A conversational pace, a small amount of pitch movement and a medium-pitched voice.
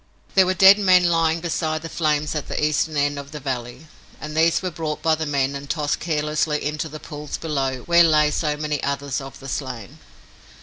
No: fast, 210 wpm; narrow, 2.3 semitones; medium, 150 Hz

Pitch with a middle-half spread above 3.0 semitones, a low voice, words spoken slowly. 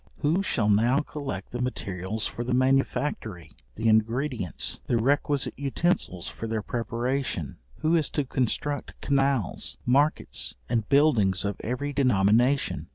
Yes: average, 4.5 semitones; low, 125 Hz; slow, 130 wpm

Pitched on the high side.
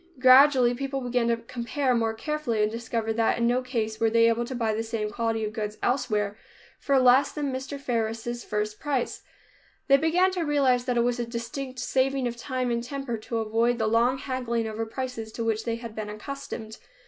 Yes: high, 235 Hz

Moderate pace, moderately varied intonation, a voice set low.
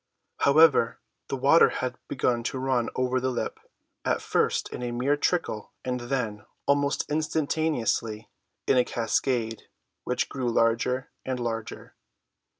No: slow, 130 wpm; average, 3.1 semitones; low, 125 Hz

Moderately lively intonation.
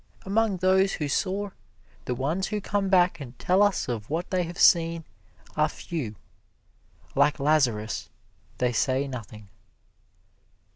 No: wide, 6.4 semitones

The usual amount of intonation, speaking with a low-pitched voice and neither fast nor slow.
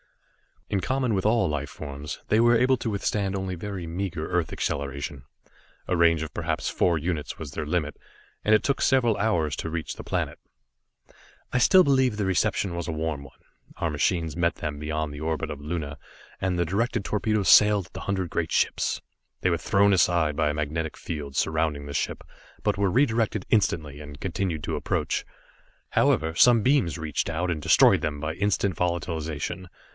Yes: average, 4.8 semitones; very low, 85 Hz; average, 185 wpm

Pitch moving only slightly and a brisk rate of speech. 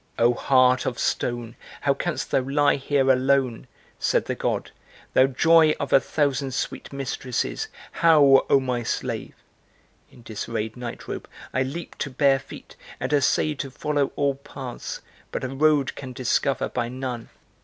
No: narrow, 2.0 semitones; average, 155 wpm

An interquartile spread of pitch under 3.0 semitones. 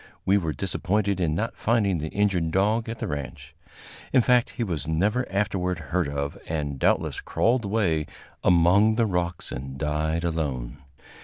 No: average, 5.1 semitones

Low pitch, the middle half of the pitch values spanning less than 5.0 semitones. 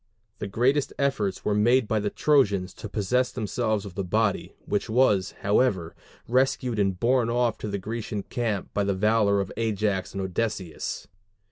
Yes: low, 105 Hz; average, 3.2 semitones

